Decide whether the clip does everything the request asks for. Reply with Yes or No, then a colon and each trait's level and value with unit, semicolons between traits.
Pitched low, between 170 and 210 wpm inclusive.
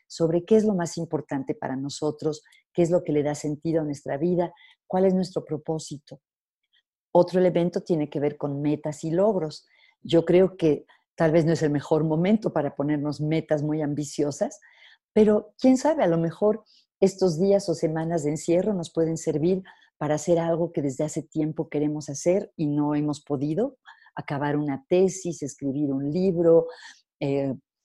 No: medium, 160 Hz; average, 175 wpm